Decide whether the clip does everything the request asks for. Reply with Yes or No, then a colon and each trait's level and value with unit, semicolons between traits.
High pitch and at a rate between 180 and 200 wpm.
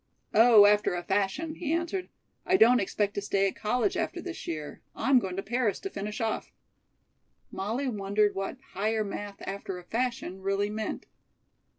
No: high, 210 Hz; average, 170 wpm